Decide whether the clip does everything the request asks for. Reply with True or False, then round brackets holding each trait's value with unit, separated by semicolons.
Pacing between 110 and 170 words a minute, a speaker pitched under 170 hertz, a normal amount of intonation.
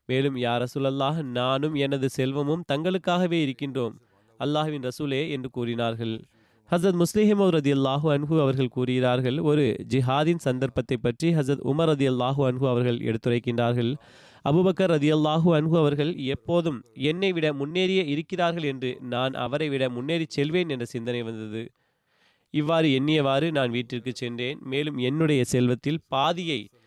True (130 wpm; 135 Hz; 3.8 semitones)